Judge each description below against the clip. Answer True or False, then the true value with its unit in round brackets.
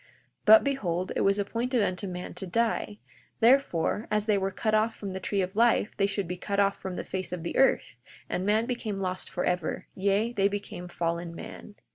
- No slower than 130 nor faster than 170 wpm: False (200 wpm)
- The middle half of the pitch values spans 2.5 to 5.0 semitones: True (3.2 semitones)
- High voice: True (200 Hz)